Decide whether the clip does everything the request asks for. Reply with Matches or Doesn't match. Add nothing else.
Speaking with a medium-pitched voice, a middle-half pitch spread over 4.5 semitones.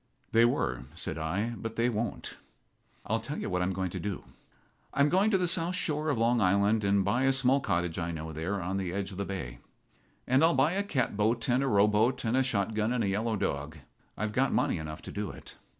Doesn't match